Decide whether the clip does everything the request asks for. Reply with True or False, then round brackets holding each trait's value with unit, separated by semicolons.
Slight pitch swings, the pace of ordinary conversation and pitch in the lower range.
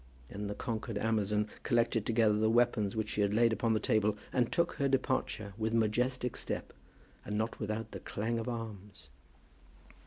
True (2.0 semitones; 175 wpm; 110 Hz)